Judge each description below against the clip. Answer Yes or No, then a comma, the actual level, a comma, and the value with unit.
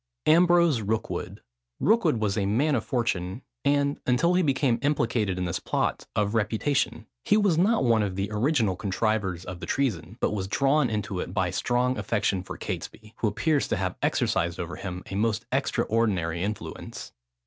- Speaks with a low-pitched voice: Yes, low, 110 Hz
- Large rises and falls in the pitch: Yes, wide, 6.0 semitones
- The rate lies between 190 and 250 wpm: No, average, 175 wpm